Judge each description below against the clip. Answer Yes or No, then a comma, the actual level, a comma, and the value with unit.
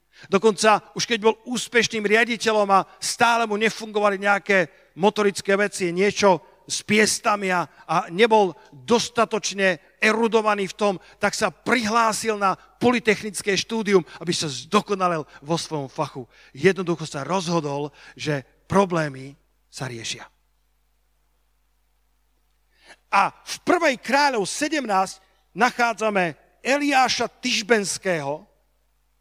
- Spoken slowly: Yes, slow, 105 wpm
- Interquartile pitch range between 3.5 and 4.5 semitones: Yes, average, 4.2 semitones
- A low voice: No, high, 200 Hz